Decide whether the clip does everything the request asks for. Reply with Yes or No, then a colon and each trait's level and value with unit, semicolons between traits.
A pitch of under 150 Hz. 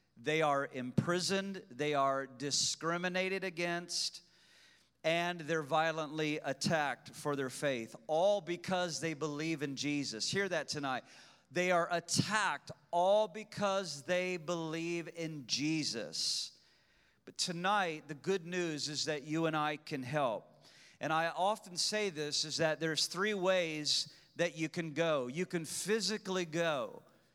No: medium, 165 Hz